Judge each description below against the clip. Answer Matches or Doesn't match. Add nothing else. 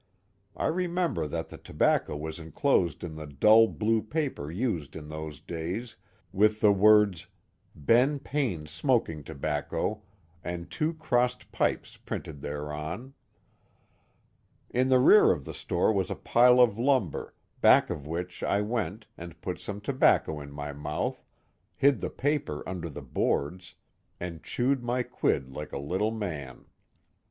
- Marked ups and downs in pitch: Matches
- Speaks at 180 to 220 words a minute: Doesn't match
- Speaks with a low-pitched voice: Matches